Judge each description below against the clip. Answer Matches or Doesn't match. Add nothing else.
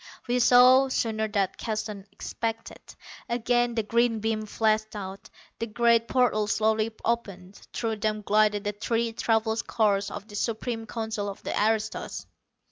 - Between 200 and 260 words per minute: Doesn't match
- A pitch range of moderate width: Doesn't match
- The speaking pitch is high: Matches